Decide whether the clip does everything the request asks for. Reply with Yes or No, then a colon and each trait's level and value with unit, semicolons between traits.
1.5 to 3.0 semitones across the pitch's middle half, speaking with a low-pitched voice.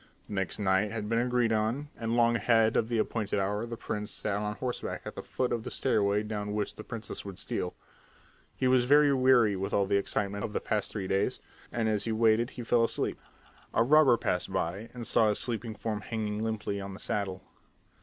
Yes: narrow, 2.4 semitones; low, 110 Hz